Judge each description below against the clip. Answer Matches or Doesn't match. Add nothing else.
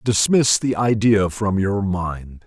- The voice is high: Doesn't match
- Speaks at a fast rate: Doesn't match